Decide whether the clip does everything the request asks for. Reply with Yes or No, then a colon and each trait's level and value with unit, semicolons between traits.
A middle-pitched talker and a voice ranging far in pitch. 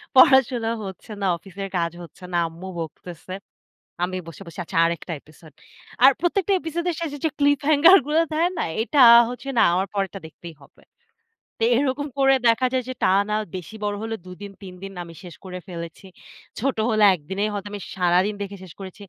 No: high, 200 Hz; wide, 6.8 semitones